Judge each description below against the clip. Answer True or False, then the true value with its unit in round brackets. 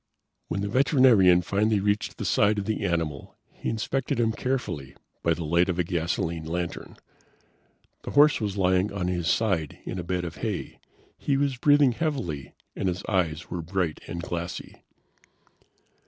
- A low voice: True (95 Hz)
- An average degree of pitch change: True (4.5 semitones)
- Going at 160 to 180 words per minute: True (165 wpm)